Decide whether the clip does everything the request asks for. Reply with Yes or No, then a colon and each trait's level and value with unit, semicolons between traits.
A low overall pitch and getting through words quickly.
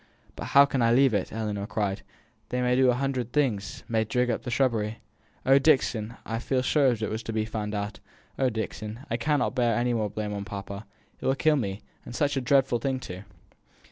Yes: low, 120 Hz; fast, 225 wpm